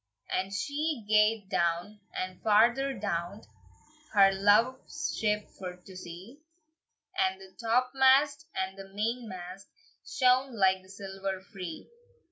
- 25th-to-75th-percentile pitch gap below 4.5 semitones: No, average, 4.8 semitones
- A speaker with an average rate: No, slow, 115 wpm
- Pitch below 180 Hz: No, high, 205 Hz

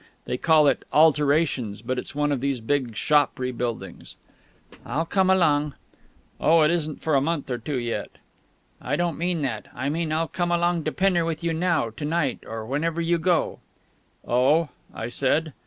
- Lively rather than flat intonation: No, average, 4.4 semitones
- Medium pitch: Yes, medium, 150 Hz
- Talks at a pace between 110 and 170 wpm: No, average, 180 wpm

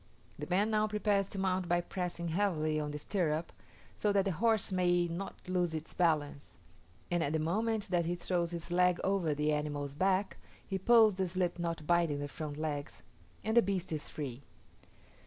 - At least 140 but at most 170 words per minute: No, average, 190 wpm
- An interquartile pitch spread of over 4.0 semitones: No, average, 3.7 semitones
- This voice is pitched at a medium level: Yes, medium, 175 Hz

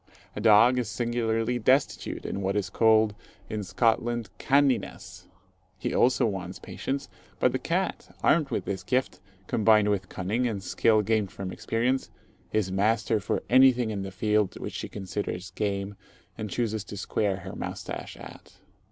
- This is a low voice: Yes, low, 110 Hz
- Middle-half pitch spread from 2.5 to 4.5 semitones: Yes, average, 3.5 semitones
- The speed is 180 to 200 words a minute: No, average, 155 wpm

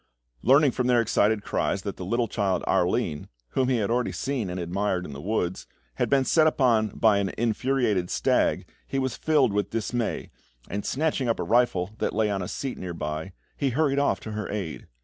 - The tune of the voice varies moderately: Yes, average, 5.0 semitones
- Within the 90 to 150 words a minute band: No, fast, 205 wpm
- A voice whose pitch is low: Yes, low, 110 Hz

